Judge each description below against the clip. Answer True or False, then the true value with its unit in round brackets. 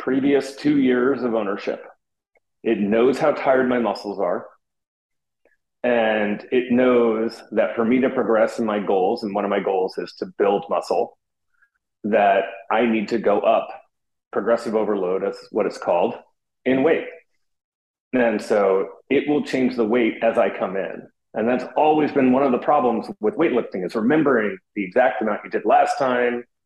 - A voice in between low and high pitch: False (125 Hz)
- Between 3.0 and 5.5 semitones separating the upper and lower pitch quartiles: True (3.8 semitones)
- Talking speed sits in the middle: True (170 wpm)